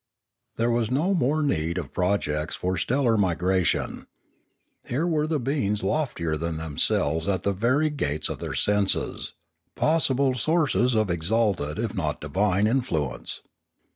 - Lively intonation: Yes, wide, 7.7 semitones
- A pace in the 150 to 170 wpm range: No, average, 140 wpm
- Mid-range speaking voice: No, low, 105 Hz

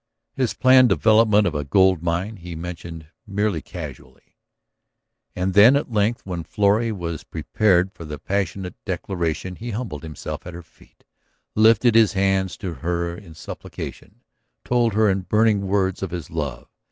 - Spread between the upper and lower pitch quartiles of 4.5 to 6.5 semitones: No, average, 3.8 semitones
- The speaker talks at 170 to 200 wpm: No, average, 155 wpm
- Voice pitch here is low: Yes, very low, 95 Hz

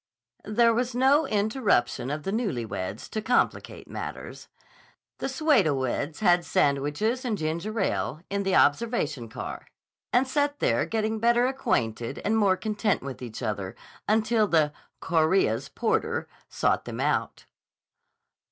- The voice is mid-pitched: No, high, 205 Hz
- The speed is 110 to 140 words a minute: Yes, slow, 135 wpm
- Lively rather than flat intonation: Yes, wide, 8.4 semitones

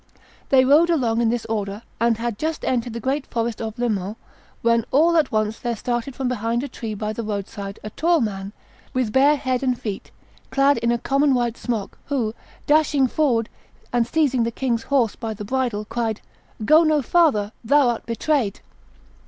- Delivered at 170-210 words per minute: Yes, average, 195 wpm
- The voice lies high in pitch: Yes, high, 235 Hz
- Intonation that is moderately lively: Yes, average, 3.8 semitones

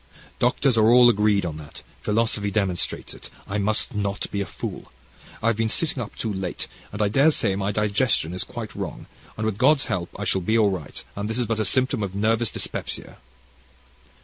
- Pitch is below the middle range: Yes, low, 105 Hz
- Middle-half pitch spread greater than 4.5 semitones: No, narrow, 2.6 semitones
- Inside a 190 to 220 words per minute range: Yes, average, 200 wpm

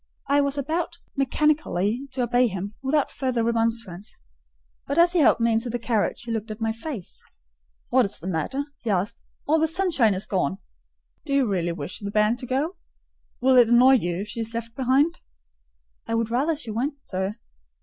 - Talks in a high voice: Yes, high, 235 Hz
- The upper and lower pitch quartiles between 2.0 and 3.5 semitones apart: No, average, 4.7 semitones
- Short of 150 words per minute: No, average, 195 wpm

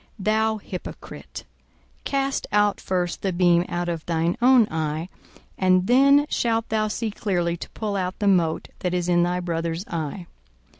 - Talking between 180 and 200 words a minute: No, average, 160 wpm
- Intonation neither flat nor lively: Yes, average, 3.9 semitones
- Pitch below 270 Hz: Yes, medium, 185 Hz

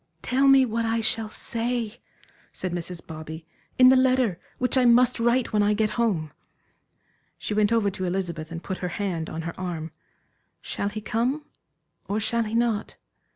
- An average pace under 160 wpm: No, average, 175 wpm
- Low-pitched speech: No, high, 215 Hz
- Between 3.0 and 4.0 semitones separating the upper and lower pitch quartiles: No, average, 4.8 semitones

